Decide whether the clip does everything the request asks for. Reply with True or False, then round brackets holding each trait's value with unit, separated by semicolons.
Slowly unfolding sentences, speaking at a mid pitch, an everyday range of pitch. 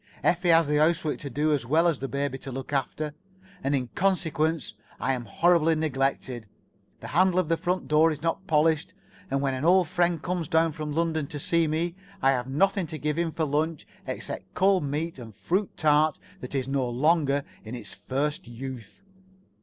False (200 wpm; 150 Hz; 3.4 semitones)